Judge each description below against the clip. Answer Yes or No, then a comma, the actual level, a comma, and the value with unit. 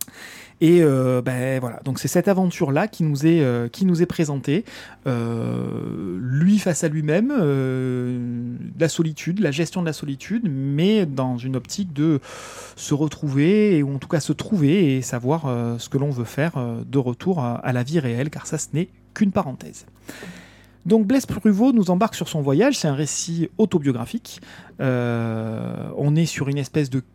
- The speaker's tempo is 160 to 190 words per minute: Yes, average, 185 wpm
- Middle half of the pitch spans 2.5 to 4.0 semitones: No, wide, 5.4 semitones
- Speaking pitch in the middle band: Yes, medium, 150 Hz